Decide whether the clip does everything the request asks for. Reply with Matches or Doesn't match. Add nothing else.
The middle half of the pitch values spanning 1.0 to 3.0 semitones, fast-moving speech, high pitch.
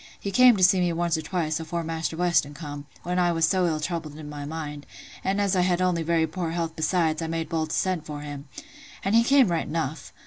Doesn't match